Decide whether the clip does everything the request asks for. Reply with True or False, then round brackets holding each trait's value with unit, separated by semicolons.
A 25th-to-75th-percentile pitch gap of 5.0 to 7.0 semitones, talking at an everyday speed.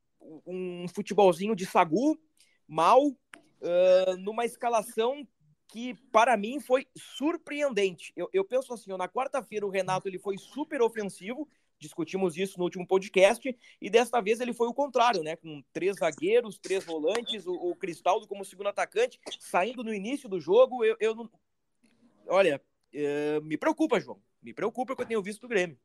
True (5.3 semitones; 165 wpm)